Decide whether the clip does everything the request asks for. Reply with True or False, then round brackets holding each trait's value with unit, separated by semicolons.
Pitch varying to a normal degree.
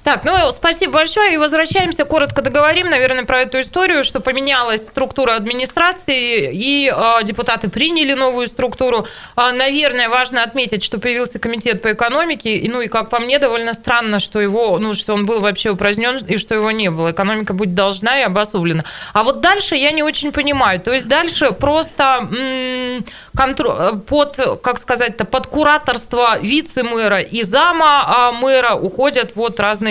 True (4.1 semitones)